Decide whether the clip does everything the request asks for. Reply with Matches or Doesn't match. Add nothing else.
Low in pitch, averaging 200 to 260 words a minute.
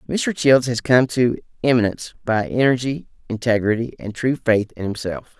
Doesn't match